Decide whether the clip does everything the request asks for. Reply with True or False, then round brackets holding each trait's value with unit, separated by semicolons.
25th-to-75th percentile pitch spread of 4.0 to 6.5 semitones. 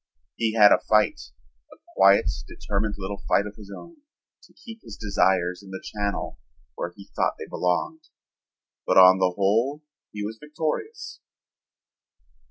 False (2.7 semitones)